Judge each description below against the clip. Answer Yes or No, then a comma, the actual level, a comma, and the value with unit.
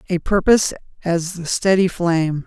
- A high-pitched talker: No, medium, 175 Hz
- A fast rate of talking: No, average, 145 wpm